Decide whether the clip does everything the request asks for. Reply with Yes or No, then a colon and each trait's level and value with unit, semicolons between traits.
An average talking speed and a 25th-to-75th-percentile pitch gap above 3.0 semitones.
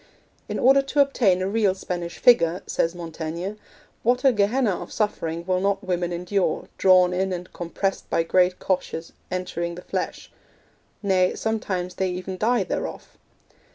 No: average, 155 wpm; narrow, 2.6 semitones